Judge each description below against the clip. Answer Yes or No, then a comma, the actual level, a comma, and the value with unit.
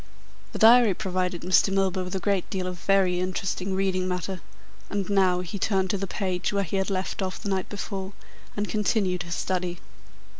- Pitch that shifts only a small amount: Yes, narrow, 1.4 semitones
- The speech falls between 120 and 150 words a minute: No, average, 190 wpm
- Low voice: No, high, 190 Hz